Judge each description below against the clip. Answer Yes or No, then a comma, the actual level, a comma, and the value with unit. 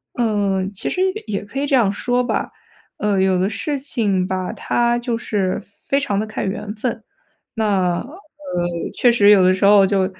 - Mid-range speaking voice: No, high, 205 Hz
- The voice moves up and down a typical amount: Yes, average, 3.8 semitones